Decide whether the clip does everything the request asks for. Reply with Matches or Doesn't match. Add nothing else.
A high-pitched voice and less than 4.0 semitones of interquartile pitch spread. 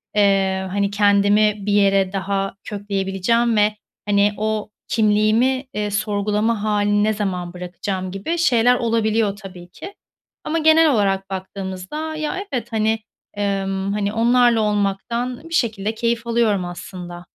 Matches